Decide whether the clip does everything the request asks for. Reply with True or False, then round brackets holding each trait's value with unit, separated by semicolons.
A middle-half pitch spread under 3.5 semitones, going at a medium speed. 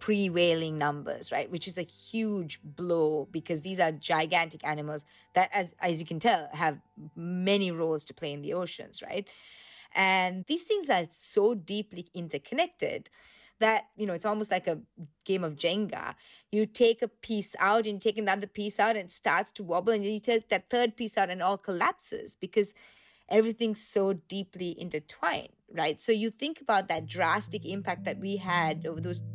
False (4.3 semitones; 185 wpm)